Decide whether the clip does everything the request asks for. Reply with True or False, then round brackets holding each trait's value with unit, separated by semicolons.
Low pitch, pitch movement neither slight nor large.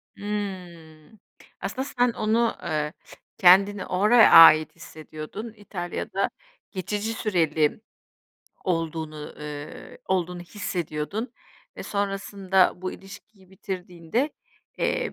False (185 Hz; 4.3 semitones)